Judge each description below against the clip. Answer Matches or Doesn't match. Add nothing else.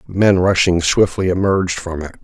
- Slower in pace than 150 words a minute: Doesn't match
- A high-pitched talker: Doesn't match